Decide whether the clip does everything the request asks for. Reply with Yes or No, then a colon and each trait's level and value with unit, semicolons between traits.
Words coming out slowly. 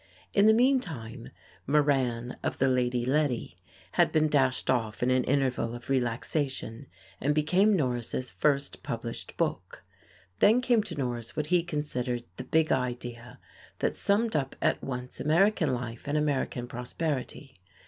No: average, 145 wpm